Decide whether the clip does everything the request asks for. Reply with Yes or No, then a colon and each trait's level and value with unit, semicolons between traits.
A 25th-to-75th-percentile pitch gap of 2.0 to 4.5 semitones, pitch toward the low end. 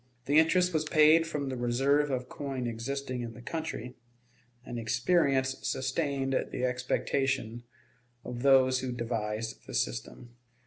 Yes: average, 2.7 semitones; low, 130 Hz